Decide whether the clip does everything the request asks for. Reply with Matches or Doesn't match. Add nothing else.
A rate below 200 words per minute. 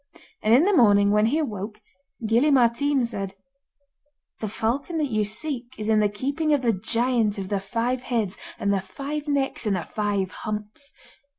Matches